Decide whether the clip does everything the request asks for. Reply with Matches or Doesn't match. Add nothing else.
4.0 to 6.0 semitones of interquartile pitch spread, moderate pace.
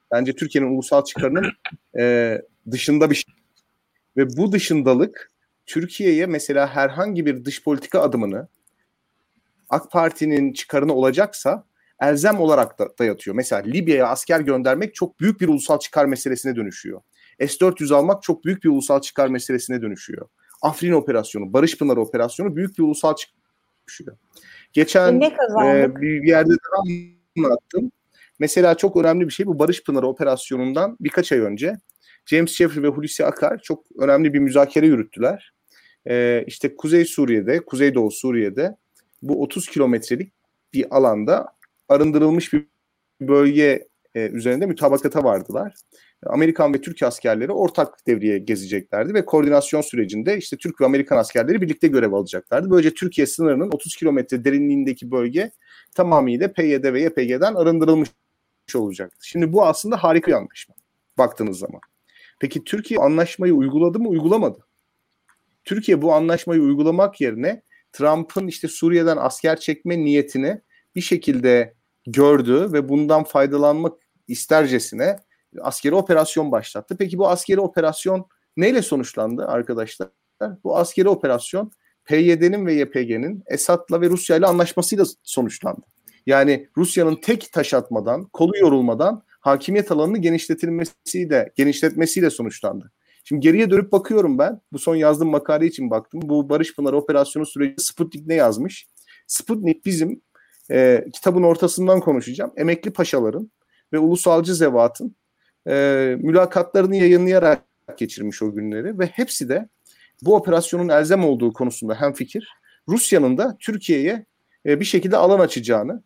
Matches